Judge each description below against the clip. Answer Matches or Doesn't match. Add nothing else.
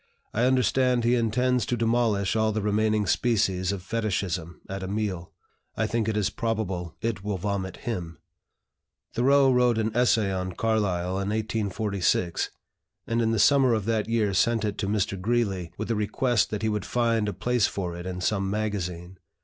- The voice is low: Matches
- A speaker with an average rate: Matches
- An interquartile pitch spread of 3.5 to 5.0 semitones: Doesn't match